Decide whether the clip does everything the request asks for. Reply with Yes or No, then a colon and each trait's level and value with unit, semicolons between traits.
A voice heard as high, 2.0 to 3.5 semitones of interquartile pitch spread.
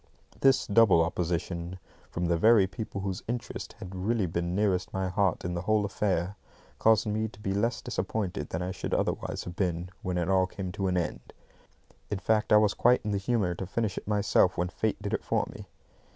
No: very low, 95 Hz; average, 3.0 semitones